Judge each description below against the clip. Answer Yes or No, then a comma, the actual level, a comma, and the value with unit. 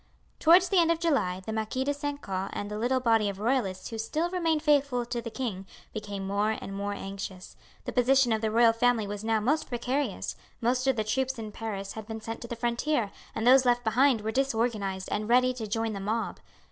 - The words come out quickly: Yes, fast, 225 wpm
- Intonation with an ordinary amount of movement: Yes, average, 3.8 semitones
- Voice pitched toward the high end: Yes, high, 230 Hz